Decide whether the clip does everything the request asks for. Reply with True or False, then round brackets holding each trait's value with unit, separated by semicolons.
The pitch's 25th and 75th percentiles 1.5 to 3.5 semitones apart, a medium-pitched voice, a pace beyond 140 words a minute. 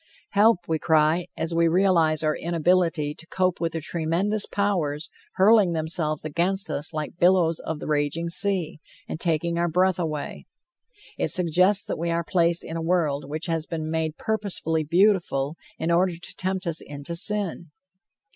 True (2.6 semitones; 170 Hz; 165 wpm)